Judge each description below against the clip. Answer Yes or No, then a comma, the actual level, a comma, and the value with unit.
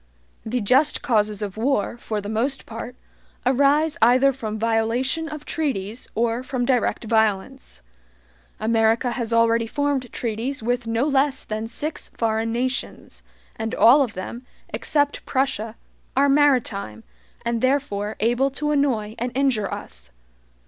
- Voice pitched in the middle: No, high, 235 Hz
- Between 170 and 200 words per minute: No, slow, 135 wpm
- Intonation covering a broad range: No, average, 3.7 semitones